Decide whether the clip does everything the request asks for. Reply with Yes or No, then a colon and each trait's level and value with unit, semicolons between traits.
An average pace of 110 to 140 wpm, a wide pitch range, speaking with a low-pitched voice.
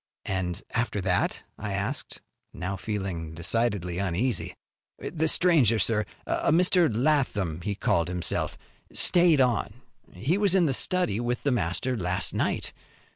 Yes: slow, 135 wpm; wide, 7.1 semitones; low, 110 Hz